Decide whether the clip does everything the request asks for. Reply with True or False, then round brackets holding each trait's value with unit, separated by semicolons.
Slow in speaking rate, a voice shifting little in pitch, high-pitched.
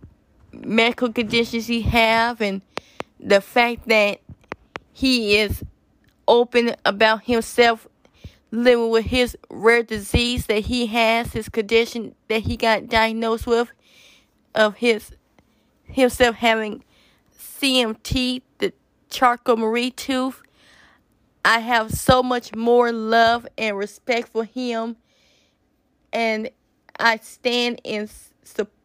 True (110 wpm; 1.5 semitones; 230 Hz)